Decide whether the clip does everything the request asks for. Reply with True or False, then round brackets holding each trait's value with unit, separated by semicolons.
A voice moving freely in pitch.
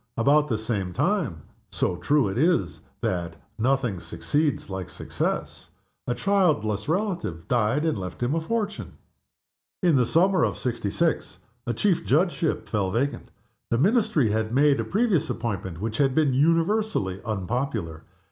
True (7.7 semitones)